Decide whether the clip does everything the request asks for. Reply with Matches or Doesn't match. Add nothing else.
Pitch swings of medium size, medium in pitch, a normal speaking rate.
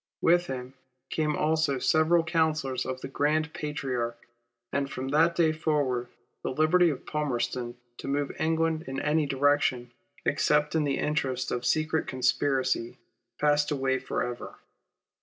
Matches